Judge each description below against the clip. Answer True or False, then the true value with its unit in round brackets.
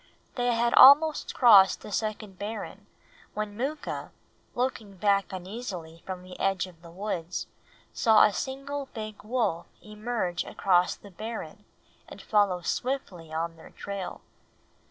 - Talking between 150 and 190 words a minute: False (135 wpm)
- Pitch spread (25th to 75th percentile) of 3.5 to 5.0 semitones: True (4.4 semitones)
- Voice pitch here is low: False (205 Hz)